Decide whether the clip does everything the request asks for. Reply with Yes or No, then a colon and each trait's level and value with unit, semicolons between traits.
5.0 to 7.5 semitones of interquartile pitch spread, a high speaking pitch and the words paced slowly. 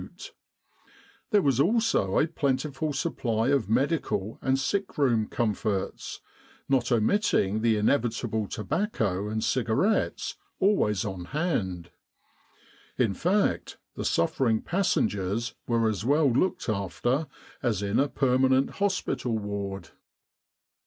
No: wide, 5.4 semitones; low, 120 Hz; slow, 110 wpm